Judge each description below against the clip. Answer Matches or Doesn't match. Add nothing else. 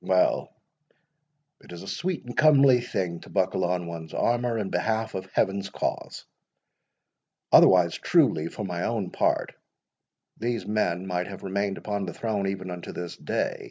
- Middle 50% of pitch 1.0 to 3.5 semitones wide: Doesn't match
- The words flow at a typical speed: Matches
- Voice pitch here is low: Matches